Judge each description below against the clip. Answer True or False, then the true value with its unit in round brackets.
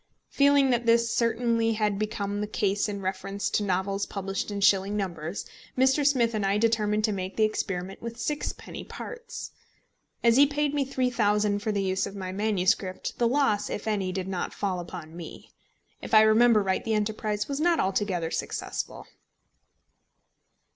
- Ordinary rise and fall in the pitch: True (3.1 semitones)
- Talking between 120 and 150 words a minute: False (170 wpm)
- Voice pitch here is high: True (210 Hz)